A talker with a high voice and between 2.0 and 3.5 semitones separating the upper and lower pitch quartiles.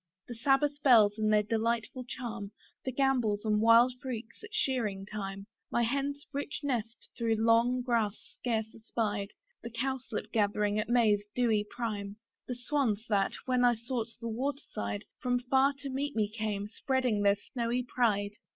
Yes: high, 230 Hz; average, 3.1 semitones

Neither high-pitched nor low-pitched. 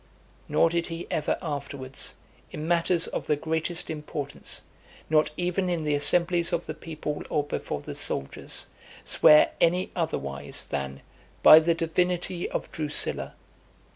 Yes: medium, 160 Hz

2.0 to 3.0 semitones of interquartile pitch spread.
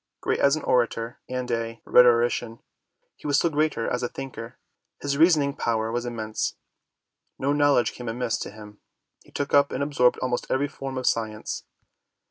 No: average, 3.5 semitones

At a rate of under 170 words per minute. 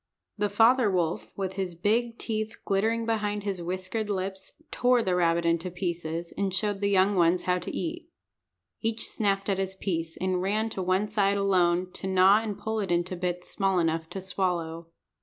No: average, 185 wpm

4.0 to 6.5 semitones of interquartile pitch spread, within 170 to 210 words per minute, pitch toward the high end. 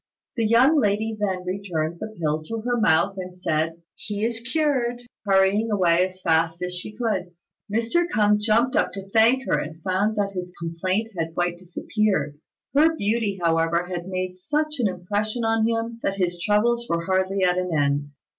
Yes: average, 4.3 semitones; average, 180 wpm; high, 195 Hz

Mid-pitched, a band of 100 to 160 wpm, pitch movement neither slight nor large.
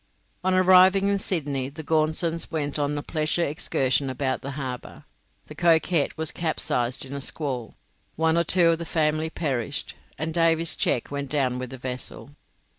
No: medium, 155 Hz; average, 170 wpm; average, 3.5 semitones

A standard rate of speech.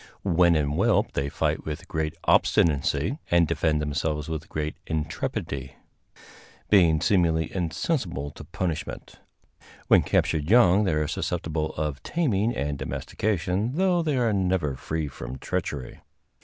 No: slow, 130 wpm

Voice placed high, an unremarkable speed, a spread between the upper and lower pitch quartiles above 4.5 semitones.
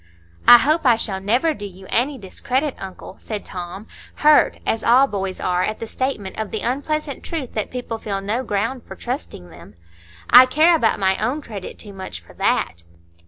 Yes: high, 225 Hz; average, 190 wpm; average, 5.2 semitones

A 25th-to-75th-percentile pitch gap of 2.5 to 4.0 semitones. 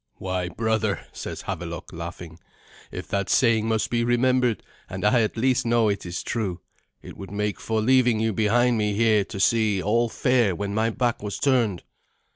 Yes: average, 3.0 semitones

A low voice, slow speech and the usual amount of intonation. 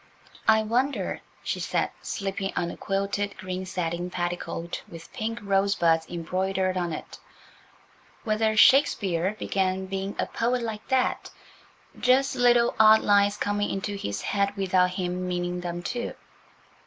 No: high, 195 Hz; slow, 130 wpm; average, 3.3 semitones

